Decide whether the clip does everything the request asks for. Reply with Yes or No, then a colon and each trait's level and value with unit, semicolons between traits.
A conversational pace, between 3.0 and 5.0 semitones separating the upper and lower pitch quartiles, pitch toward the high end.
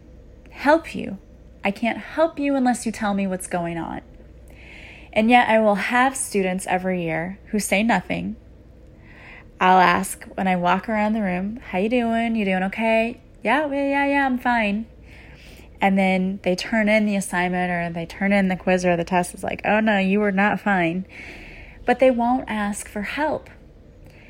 Yes: average, 180 wpm; average, 3.6 semitones; high, 205 Hz